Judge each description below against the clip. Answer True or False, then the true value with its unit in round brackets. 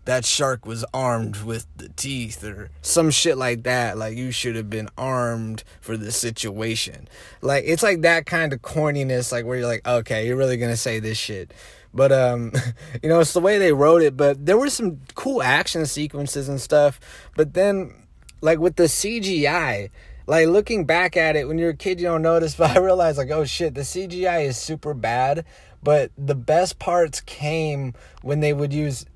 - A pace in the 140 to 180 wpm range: False (200 wpm)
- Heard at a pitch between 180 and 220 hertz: False (140 Hz)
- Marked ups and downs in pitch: True (5.7 semitones)